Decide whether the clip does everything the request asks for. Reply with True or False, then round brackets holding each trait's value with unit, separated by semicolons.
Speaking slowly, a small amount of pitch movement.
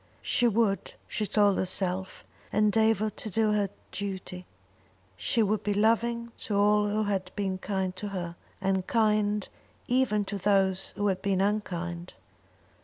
False (145 wpm; 2.0 semitones)